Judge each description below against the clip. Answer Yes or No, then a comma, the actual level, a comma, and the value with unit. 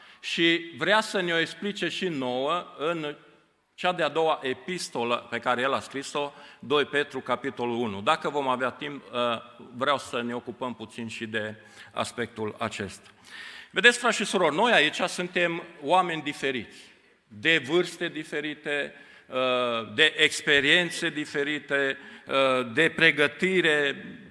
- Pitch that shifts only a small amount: No, average, 5.3 semitones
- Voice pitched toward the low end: No, medium, 145 Hz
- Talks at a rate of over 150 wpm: No, average, 130 wpm